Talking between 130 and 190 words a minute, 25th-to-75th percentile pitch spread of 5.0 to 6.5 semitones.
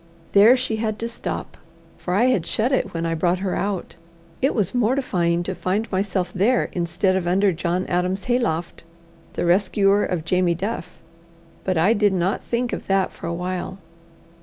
No: average, 180 wpm; average, 3.4 semitones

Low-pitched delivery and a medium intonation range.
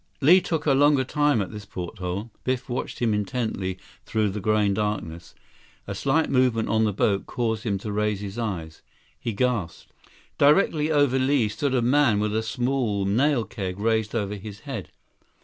Yes: low, 110 Hz; average, 4.2 semitones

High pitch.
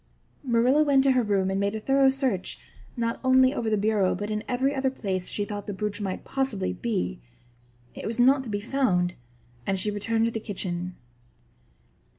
Yes: high, 220 Hz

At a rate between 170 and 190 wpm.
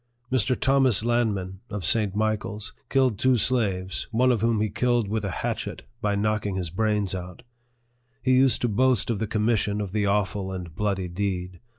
Yes: average, 180 wpm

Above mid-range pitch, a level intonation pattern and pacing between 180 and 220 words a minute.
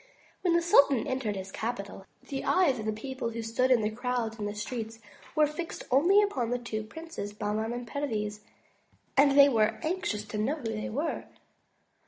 No: high, 240 Hz; average, 4.6 semitones; average, 185 wpm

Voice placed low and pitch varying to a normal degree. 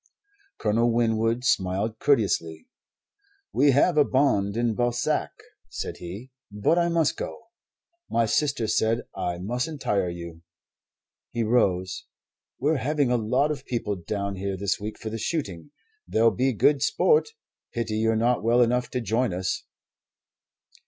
Yes: low, 115 Hz; average, 4.4 semitones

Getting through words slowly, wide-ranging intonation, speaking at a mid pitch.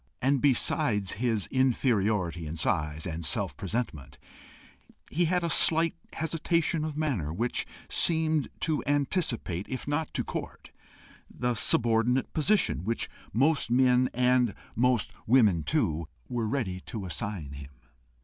No: slow, 130 wpm; wide, 7.3 semitones; low, 120 Hz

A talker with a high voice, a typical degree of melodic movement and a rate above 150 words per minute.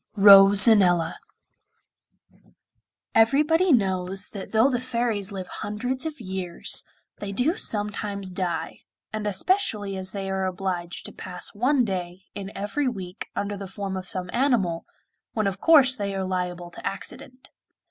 No: high, 200 Hz; average, 3.8 semitones; average, 140 wpm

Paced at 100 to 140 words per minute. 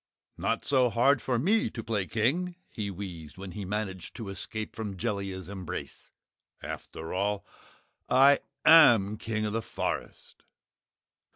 Yes: slow, 135 wpm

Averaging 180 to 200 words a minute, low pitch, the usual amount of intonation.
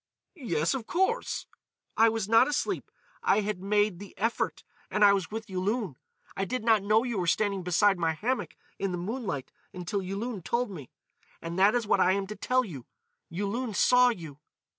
No: average, 185 wpm; high, 205 Hz; average, 3.8 semitones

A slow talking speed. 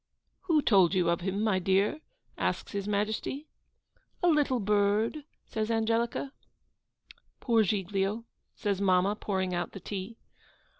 Yes: slow, 130 wpm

